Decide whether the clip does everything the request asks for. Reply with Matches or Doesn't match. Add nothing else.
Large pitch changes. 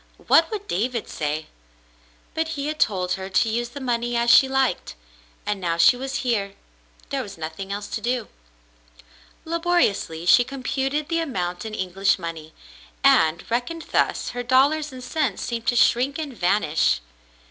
Matches